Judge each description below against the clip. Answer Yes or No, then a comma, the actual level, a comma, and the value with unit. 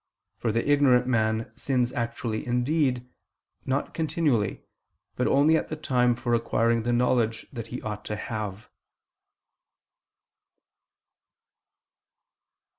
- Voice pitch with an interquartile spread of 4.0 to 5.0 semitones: No, narrow, 2.6 semitones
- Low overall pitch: Yes, low, 120 Hz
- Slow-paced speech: Yes, slow, 110 wpm